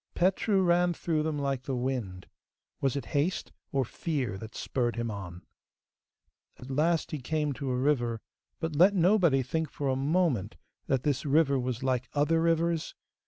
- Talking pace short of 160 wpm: No, average, 165 wpm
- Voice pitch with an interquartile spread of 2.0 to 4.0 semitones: No, average, 4.5 semitones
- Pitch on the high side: No, medium, 140 Hz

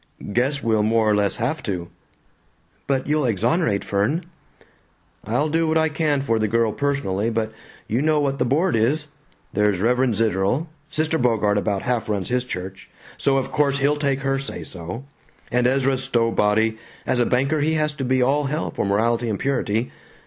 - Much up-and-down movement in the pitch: No, average, 4.6 semitones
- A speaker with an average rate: Yes, average, 180 wpm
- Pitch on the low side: Yes, low, 125 Hz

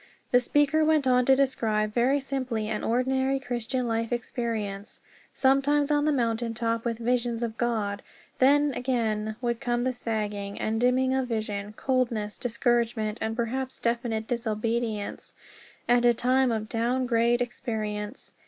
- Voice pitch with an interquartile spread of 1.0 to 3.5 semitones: Yes, narrow, 2.6 semitones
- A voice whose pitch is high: Yes, high, 240 Hz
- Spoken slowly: No, average, 145 wpm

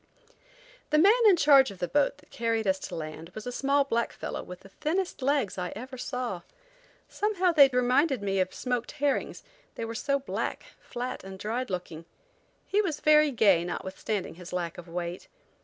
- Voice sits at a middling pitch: No, high, 240 Hz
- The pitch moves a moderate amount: No, wide, 7.1 semitones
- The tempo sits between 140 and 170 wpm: No, average, 185 wpm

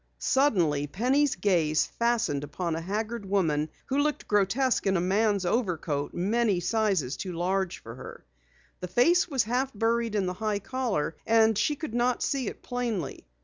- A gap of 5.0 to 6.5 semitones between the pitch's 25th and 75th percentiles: Yes, wide, 5.4 semitones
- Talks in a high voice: Yes, high, 205 Hz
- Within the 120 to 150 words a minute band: No, average, 165 wpm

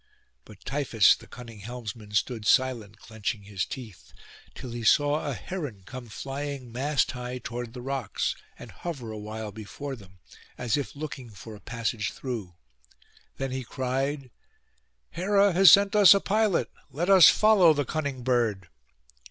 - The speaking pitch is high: No, low, 125 Hz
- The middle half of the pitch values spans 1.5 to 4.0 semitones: No, average, 4.7 semitones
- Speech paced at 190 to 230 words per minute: No, average, 150 wpm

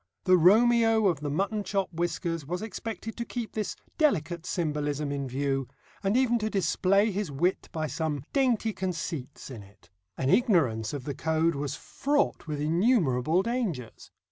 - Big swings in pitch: Yes, wide, 6.8 semitones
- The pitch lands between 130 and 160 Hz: No, medium, 175 Hz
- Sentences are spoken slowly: No, average, 160 wpm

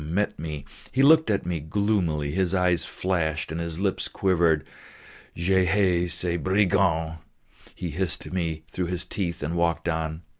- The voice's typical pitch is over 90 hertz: No, very low, 85 Hz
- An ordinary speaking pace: Yes, average, 160 wpm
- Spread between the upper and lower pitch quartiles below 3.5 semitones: Yes, average, 2.7 semitones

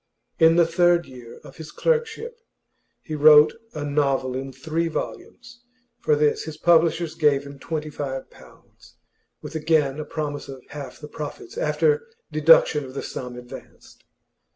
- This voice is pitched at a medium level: Yes, medium, 150 Hz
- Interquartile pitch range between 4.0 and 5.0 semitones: No, average, 3.2 semitones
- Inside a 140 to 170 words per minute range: Yes, average, 150 wpm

